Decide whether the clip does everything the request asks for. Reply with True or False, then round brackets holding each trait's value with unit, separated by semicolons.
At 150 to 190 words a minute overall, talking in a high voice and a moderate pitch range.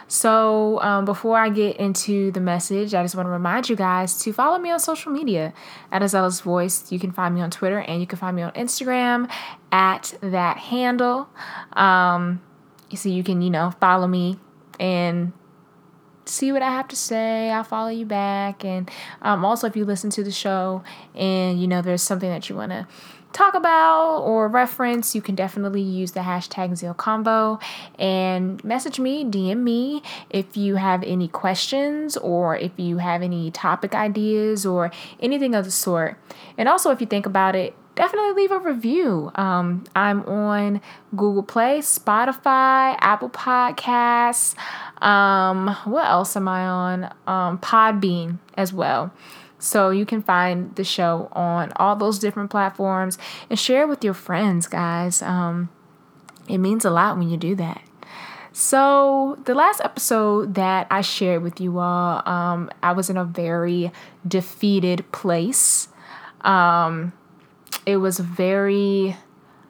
True (160 wpm; 195 Hz; 3.7 semitones)